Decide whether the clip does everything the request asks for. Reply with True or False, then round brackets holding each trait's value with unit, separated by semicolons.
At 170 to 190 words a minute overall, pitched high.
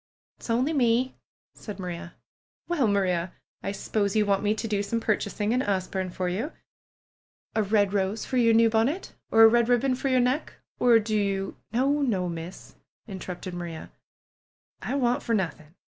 True (180 wpm; 215 Hz)